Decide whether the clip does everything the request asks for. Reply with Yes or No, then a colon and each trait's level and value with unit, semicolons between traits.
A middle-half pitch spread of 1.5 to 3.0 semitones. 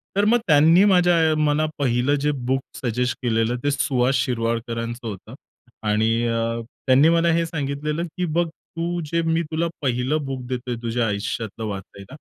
No: average, 5.3 semitones